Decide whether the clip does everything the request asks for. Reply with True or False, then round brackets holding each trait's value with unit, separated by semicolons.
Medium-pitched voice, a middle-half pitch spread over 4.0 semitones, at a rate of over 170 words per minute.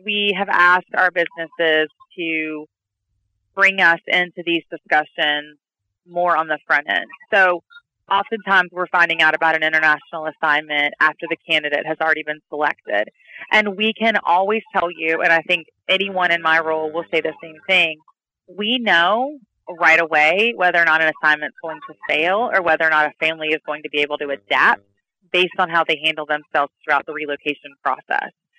False (160 Hz; 2.9 semitones; 180 wpm)